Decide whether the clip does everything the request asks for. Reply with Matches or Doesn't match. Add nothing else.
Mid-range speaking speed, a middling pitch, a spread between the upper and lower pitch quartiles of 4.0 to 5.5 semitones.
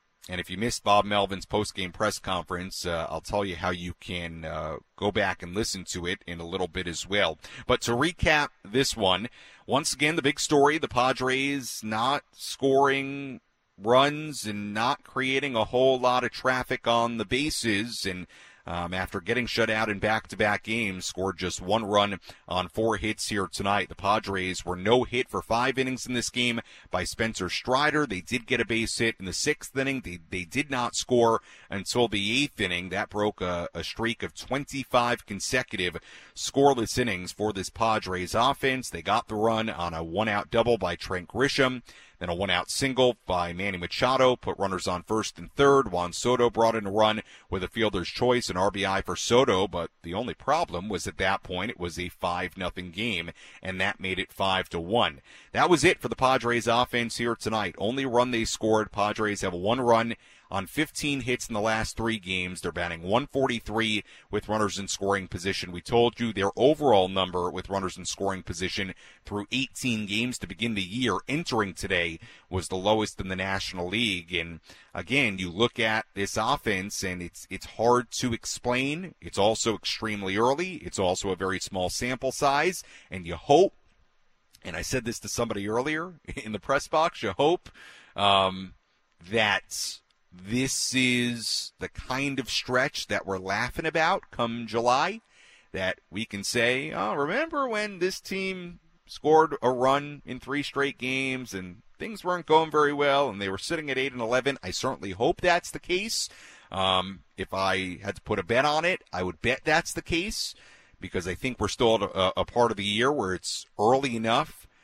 Doesn't match